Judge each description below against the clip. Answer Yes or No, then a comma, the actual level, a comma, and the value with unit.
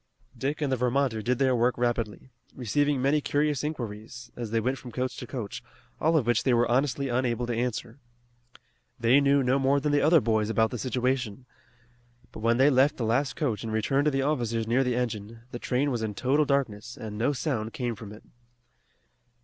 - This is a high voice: No, low, 125 Hz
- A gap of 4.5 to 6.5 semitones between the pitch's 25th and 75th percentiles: No, average, 3.1 semitones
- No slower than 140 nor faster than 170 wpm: No, fast, 205 wpm